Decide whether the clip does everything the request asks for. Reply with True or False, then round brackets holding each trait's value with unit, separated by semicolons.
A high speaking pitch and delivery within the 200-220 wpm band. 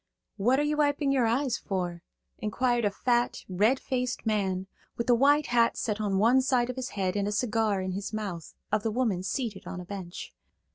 True (225 Hz; 205 wpm)